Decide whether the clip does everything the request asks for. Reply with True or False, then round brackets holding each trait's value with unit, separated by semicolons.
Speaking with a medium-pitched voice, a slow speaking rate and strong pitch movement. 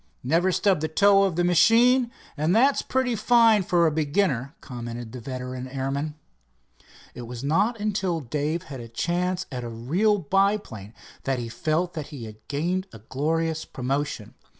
False (155 Hz; 165 wpm; 7.0 semitones)